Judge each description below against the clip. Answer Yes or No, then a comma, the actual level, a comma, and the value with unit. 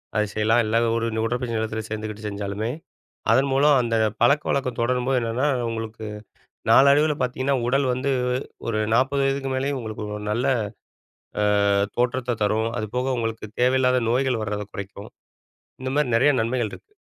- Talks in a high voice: No, low, 120 Hz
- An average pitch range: Yes, average, 3.2 semitones